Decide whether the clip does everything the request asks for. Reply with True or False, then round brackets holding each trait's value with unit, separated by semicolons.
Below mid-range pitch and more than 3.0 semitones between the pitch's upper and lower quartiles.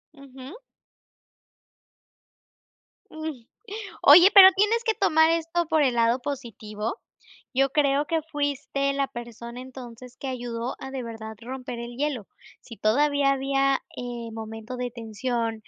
False (260 Hz; 3.5 semitones)